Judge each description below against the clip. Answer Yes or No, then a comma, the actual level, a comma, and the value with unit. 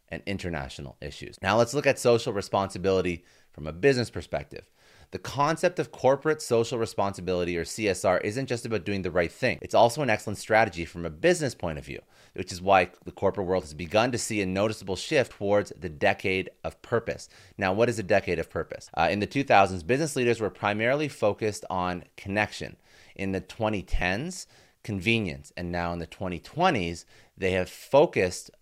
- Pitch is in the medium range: No, low, 100 Hz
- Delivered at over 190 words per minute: No, average, 180 wpm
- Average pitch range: Yes, average, 4.6 semitones